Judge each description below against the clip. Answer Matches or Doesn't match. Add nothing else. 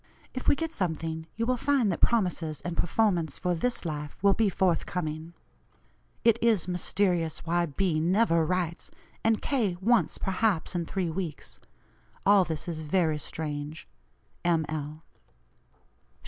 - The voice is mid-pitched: Matches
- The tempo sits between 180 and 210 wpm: Doesn't match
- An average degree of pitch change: Matches